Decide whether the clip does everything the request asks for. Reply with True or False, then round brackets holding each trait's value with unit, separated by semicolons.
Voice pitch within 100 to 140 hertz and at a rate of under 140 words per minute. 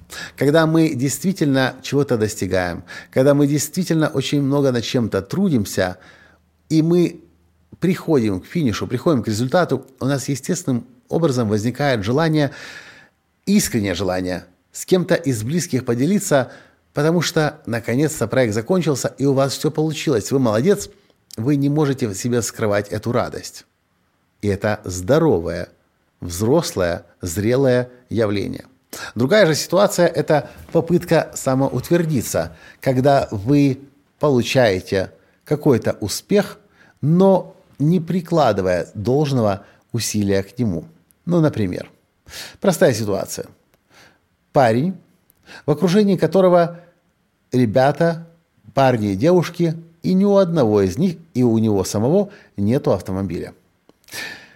True (135 Hz; 110 wpm)